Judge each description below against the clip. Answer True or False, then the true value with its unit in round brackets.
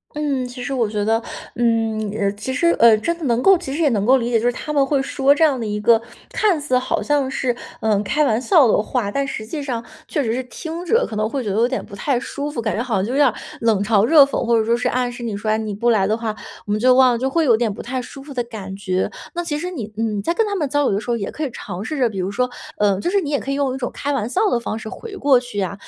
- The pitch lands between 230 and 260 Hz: True (245 Hz)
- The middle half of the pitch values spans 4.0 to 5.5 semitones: True (4.6 semitones)